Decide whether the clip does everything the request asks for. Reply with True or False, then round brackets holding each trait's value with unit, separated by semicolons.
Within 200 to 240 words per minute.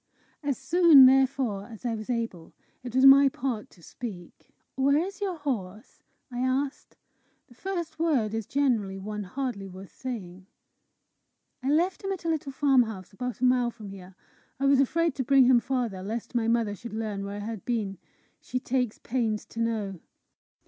False (175 wpm)